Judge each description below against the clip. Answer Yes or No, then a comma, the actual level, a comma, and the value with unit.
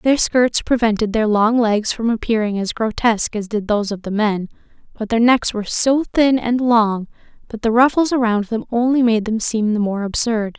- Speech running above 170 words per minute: Yes, fast, 205 wpm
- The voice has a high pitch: Yes, high, 225 Hz